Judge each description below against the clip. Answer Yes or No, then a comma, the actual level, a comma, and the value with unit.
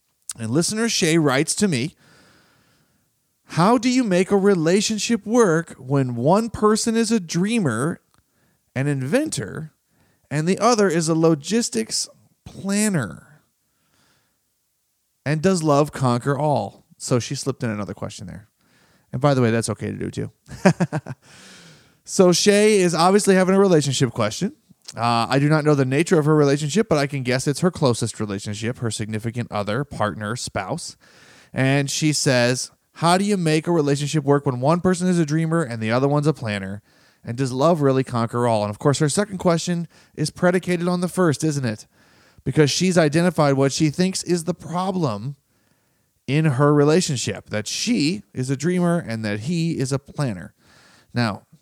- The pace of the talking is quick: No, average, 170 wpm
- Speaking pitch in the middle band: Yes, medium, 150 Hz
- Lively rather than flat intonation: Yes, wide, 6.2 semitones